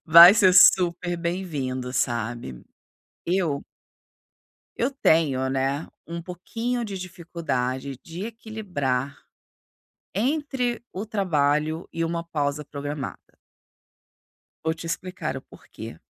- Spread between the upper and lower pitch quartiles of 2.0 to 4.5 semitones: No, average, 5.1 semitones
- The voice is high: No, medium, 165 Hz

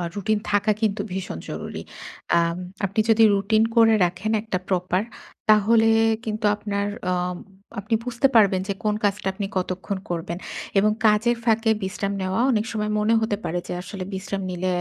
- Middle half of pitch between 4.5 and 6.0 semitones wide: No, narrow, 2.6 semitones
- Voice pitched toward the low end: No, high, 205 Hz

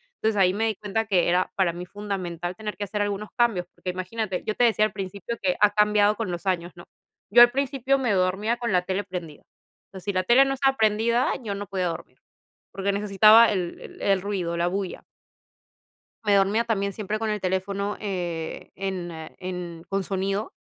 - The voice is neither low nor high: No, high, 200 Hz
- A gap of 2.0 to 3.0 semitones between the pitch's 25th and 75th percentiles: Yes, average, 2.7 semitones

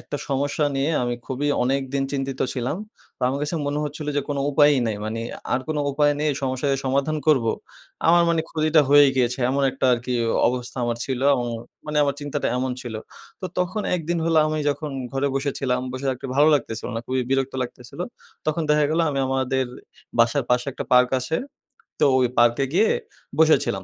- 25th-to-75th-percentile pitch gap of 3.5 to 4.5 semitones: No, average, 2.8 semitones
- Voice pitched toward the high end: No, low, 135 Hz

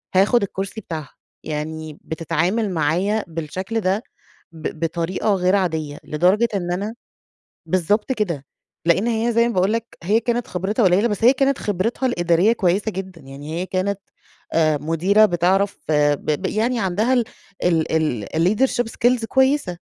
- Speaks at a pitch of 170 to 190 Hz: Yes, medium, 185 Hz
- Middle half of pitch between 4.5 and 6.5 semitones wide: Yes, average, 5.0 semitones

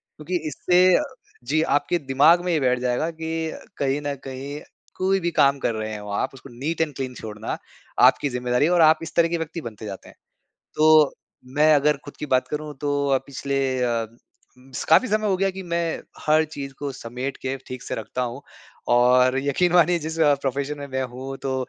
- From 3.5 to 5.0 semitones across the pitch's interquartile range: Yes, average, 3.8 semitones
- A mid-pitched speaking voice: Yes, medium, 145 Hz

